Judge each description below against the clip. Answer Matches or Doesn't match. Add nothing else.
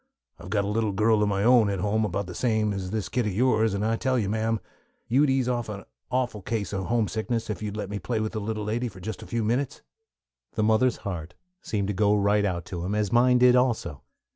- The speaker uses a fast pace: Matches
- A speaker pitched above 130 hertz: Doesn't match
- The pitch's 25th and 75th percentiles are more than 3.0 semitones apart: Doesn't match